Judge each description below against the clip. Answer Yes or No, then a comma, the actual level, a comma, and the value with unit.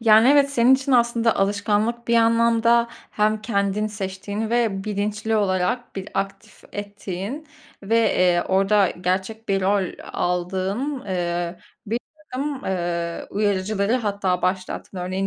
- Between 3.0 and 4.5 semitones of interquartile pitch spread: Yes, average, 3.4 semitones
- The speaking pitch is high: Yes, high, 205 Hz